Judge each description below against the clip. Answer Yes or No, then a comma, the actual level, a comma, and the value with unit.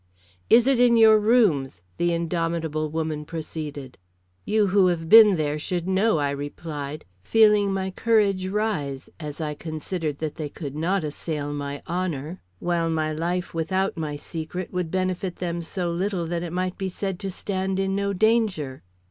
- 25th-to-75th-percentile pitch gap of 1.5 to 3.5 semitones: No, average, 3.9 semitones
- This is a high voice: No, medium, 175 Hz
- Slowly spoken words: No, average, 165 wpm